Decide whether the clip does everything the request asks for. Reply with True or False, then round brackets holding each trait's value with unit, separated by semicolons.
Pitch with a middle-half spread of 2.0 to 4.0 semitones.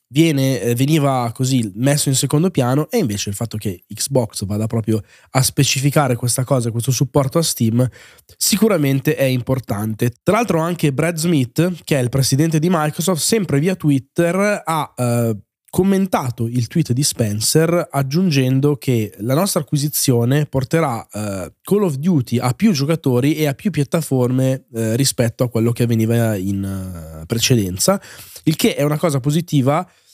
False (4.9 semitones)